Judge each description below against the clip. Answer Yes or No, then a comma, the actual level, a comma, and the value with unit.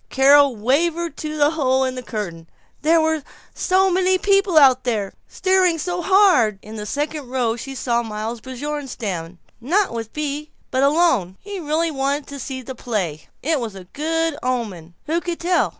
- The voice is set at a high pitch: Yes, very high, 280 Hz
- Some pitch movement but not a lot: No, wide, 5.8 semitones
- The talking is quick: No, average, 175 wpm